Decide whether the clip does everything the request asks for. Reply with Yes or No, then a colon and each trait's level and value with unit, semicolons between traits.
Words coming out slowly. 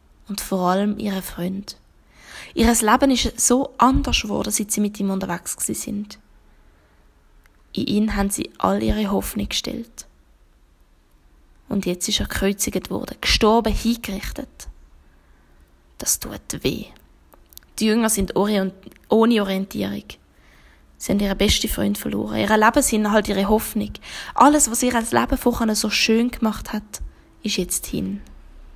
No: average, 140 wpm